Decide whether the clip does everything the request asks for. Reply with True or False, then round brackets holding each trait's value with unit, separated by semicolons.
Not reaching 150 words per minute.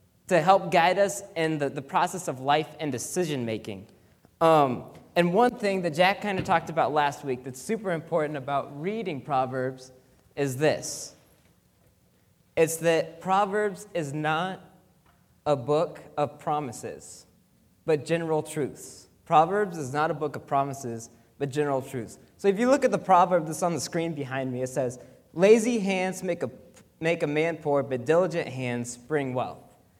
False (165 wpm)